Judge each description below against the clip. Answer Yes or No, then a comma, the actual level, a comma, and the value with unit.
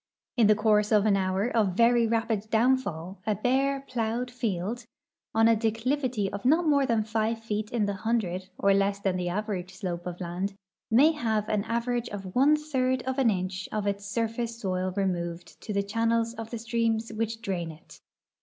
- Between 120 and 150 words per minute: No, average, 190 wpm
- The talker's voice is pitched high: Yes, high, 220 Hz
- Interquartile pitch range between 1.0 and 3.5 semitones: Yes, average, 3.0 semitones